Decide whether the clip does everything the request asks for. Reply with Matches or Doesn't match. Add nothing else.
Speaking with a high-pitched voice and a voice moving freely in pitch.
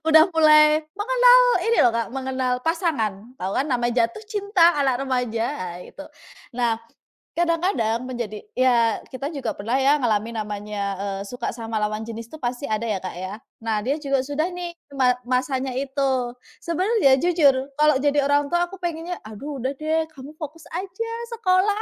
Matches